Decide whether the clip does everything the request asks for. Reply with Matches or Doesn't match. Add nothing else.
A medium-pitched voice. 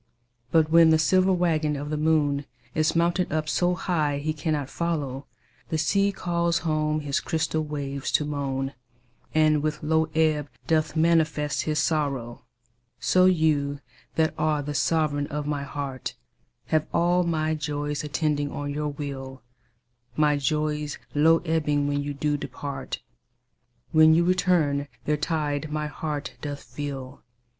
Matches